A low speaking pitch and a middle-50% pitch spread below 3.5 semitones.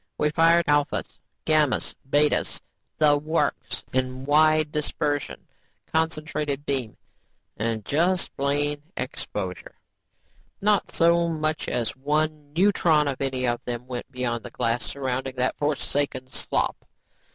No: medium, 145 Hz; average, 3.1 semitones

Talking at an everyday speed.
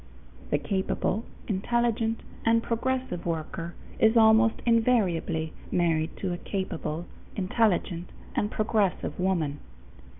No: slow, 100 wpm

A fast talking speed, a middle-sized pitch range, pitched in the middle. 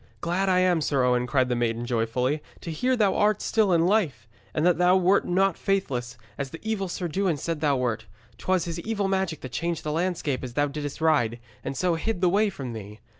No: fast, 225 wpm; wide, 6.6 semitones; medium, 165 Hz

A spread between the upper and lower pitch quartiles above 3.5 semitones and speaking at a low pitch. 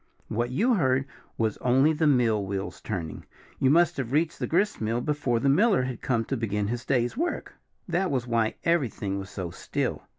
Yes: average, 5.1 semitones; low, 125 Hz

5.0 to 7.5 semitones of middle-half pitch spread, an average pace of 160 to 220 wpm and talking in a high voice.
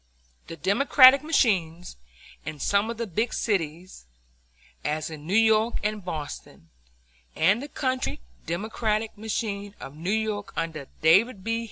No: wide, 5.4 semitones; slow, 135 wpm; high, 200 Hz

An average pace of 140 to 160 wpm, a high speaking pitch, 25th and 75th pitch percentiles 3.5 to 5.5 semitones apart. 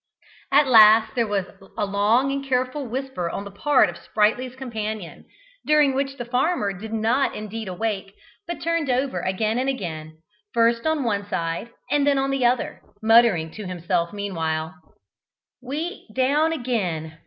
Yes: average, 155 wpm; high, 225 Hz; average, 5.0 semitones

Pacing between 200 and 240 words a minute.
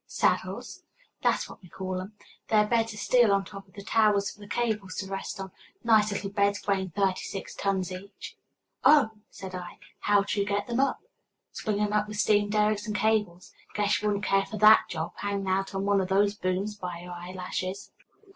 Yes: fast, 205 wpm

